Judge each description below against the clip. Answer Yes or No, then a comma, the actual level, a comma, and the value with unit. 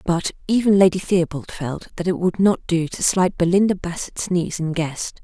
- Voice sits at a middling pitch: Yes, medium, 175 Hz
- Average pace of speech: Yes, average, 195 wpm